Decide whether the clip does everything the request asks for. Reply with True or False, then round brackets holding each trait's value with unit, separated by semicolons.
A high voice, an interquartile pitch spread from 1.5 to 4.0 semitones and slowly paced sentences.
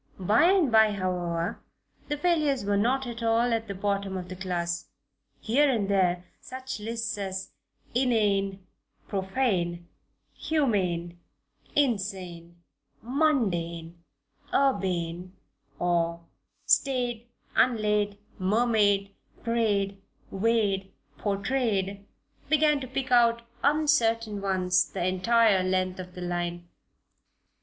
False (200 Hz; 4.4 semitones; 100 wpm)